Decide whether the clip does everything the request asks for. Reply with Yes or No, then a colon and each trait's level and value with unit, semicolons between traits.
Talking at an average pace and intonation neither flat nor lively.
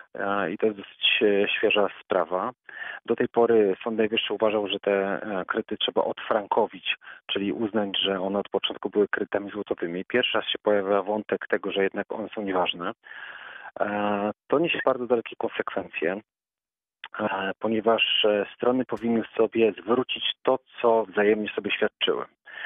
No: average, 135 wpm; narrow, 2.3 semitones